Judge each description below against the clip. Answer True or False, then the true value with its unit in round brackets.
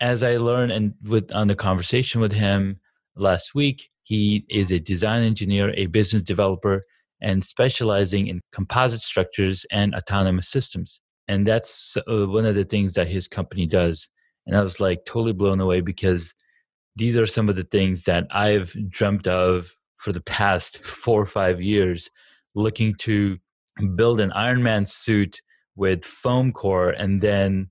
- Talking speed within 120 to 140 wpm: False (160 wpm)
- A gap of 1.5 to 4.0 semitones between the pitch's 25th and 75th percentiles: True (2.5 semitones)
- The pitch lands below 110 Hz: True (100 Hz)